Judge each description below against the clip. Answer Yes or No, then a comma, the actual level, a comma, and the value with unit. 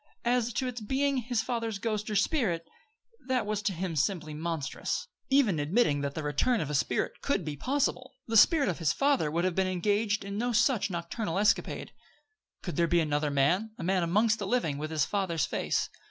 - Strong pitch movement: Yes, wide, 6.1 semitones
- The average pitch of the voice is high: Yes, high, 200 Hz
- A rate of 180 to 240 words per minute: Yes, average, 200 wpm